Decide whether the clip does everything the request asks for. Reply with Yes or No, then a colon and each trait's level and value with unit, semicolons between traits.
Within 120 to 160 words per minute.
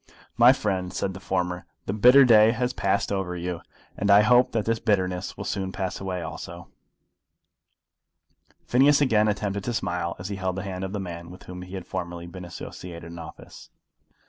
No: average, 190 wpm